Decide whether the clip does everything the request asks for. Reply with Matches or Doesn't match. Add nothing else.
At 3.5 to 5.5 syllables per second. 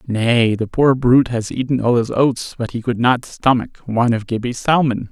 Matches